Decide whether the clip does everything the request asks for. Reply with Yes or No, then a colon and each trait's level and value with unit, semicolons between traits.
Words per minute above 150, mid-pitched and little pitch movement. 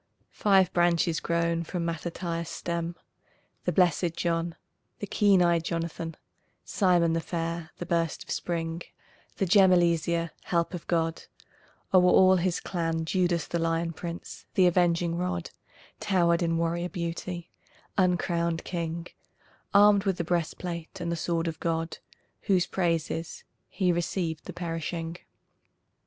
No: slow, 135 wpm; medium, 170 Hz; narrow, 1.3 semitones